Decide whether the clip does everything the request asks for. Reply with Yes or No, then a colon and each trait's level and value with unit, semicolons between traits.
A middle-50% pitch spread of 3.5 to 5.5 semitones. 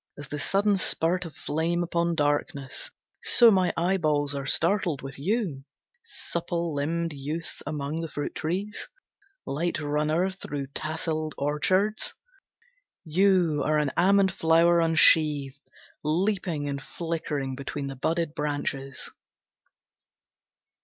No: average, 3.1 semitones